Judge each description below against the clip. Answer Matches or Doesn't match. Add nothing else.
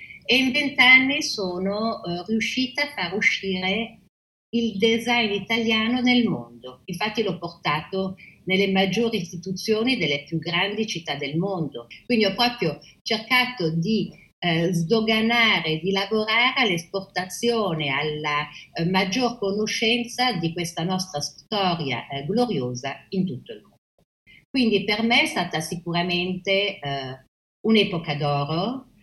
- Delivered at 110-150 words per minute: Matches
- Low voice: Doesn't match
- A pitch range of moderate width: Matches